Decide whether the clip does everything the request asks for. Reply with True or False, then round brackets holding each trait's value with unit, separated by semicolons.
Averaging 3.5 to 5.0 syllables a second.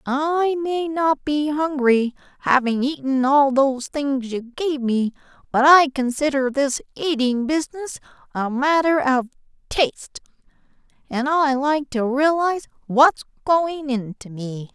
True (4.1 syllables/s)